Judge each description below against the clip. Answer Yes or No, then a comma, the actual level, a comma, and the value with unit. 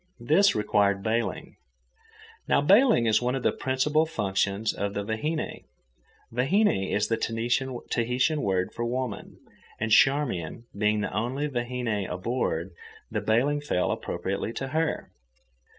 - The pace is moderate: No, slow, 125 wpm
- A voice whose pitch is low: Yes, low, 120 Hz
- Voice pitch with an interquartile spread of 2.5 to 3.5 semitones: No, average, 4.7 semitones